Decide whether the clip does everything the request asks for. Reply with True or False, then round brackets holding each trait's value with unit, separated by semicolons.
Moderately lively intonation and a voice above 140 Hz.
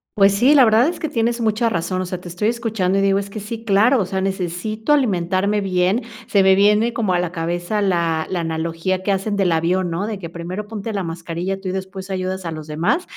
True (3.3 semitones; 190 Hz)